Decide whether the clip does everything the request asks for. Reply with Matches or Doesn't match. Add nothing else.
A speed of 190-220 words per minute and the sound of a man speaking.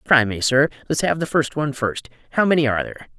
Matches